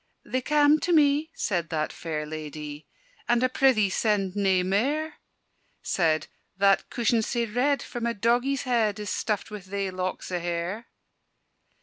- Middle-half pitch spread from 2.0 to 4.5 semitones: No, wide, 5.5 semitones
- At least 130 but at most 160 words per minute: Yes, average, 155 wpm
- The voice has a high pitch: Yes, high, 210 Hz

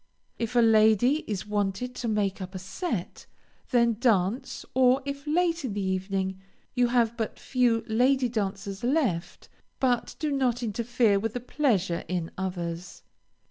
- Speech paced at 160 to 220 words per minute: No, average, 150 wpm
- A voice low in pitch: No, high, 225 Hz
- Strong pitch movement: No, average, 4.5 semitones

